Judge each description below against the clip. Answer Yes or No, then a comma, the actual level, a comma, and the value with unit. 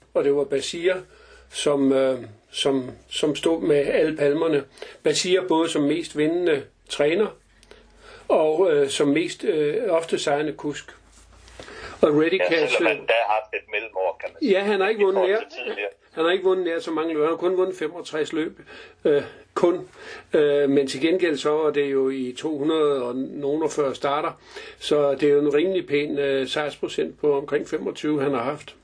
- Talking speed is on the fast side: No, average, 160 wpm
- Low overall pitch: No, medium, 155 Hz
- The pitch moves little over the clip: No, average, 4.7 semitones